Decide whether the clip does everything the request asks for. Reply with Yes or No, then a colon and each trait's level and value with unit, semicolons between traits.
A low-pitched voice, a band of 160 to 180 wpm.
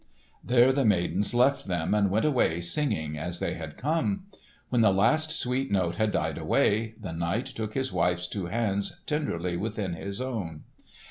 Yes: low, 105 Hz; average, 175 wpm